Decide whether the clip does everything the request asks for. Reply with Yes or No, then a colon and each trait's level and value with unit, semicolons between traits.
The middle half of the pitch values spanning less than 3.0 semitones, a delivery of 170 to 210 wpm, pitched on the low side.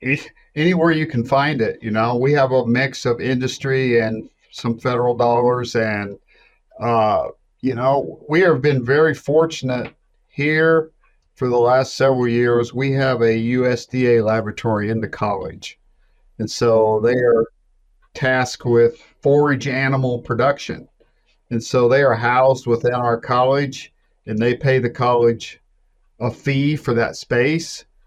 No: narrow, 2.4 semitones; average, 145 wpm; low, 125 Hz